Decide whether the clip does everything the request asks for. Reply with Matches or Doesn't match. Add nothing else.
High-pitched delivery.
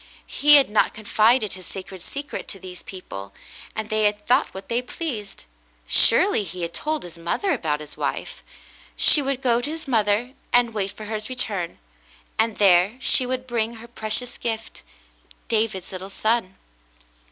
Matches